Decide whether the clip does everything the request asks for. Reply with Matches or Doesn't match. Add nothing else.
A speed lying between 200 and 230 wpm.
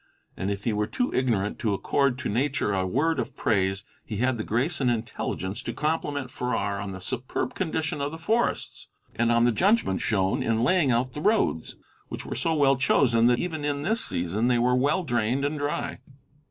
Matches